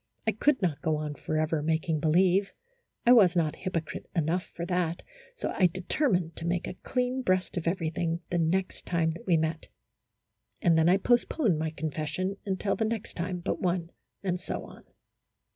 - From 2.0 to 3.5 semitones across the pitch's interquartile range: Yes, average, 2.9 semitones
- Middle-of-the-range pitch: Yes, medium, 175 Hz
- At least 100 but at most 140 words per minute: No, average, 175 wpm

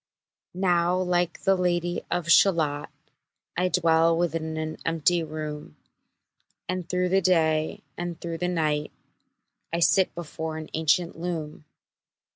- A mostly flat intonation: Yes, narrow, 1.9 semitones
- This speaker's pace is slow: Yes, slow, 125 wpm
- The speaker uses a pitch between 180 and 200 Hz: No, medium, 170 Hz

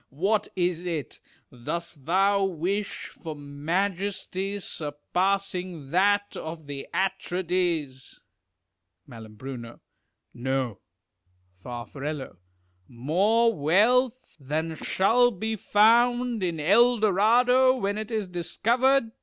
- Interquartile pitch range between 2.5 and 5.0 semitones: No, wide, 5.5 semitones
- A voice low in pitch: No, high, 190 Hz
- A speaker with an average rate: No, slow, 90 wpm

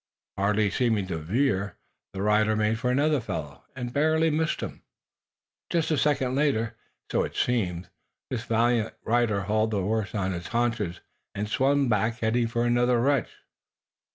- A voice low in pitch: Yes, low, 115 Hz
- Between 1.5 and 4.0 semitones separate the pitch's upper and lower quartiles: Yes, average, 3.5 semitones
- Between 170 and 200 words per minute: No, average, 155 wpm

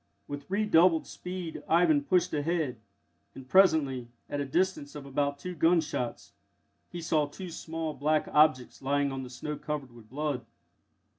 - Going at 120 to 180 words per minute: Yes, average, 150 wpm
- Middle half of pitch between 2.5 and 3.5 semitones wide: Yes, average, 3.1 semitones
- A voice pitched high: No, medium, 150 Hz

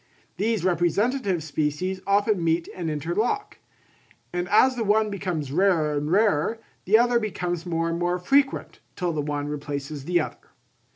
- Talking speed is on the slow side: No, average, 155 wpm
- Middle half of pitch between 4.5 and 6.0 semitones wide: Yes, average, 4.9 semitones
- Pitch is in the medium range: Yes, medium, 175 Hz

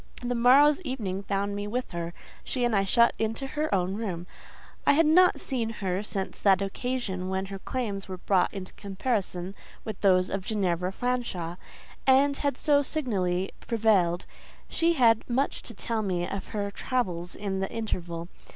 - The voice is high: Yes, high, 205 Hz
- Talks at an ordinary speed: Yes, average, 165 wpm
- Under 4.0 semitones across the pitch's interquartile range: No, average, 4.8 semitones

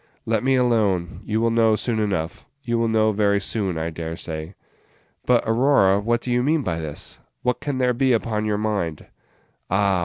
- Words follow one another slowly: No, average, 190 wpm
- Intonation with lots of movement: No, average, 3.8 semitones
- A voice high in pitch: No, low, 110 Hz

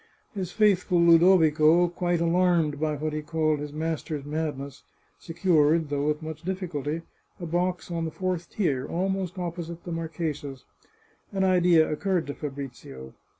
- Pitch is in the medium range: Yes, medium, 165 Hz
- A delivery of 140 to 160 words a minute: Yes, average, 150 wpm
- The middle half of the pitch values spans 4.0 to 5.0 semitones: No, average, 2.8 semitones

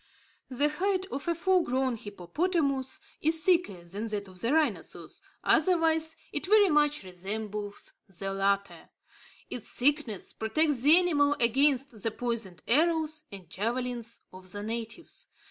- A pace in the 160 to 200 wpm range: No, slow, 135 wpm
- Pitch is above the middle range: Yes, very high, 250 Hz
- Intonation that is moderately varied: No, wide, 7.3 semitones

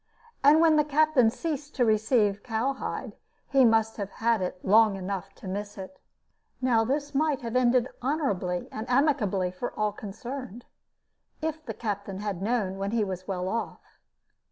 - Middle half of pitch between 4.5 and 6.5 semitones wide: Yes, average, 5.2 semitones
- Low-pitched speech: No, high, 225 Hz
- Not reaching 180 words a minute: Yes, average, 160 wpm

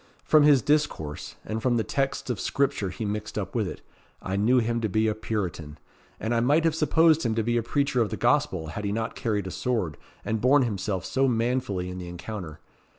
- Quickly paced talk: Yes, fast, 220 wpm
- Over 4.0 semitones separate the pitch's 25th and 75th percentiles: Yes, average, 4.6 semitones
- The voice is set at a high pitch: No, low, 115 Hz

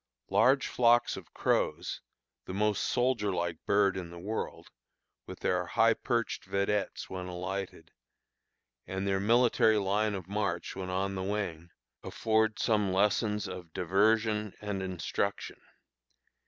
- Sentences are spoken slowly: Yes, slow, 130 wpm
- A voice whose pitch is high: No, low, 100 Hz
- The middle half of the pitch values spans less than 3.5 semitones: Yes, narrow, 2.6 semitones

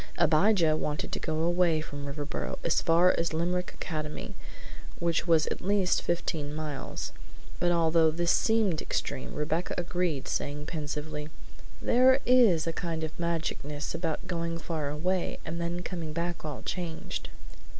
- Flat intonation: Yes, narrow, 2.3 semitones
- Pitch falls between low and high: Yes, medium, 165 Hz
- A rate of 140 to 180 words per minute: Yes, average, 150 wpm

